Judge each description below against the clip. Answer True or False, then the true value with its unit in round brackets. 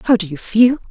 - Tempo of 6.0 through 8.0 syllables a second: True (6.1 syllables/s)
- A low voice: False (215 Hz)